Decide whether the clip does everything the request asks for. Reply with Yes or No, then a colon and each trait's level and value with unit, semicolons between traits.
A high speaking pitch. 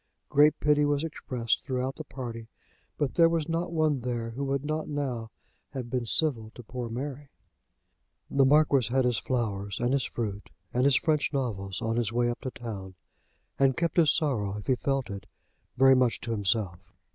No: low, 130 Hz